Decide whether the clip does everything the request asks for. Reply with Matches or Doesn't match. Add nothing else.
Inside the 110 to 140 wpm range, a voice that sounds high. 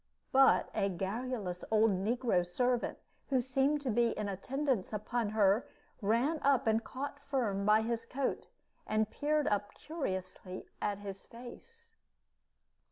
Matches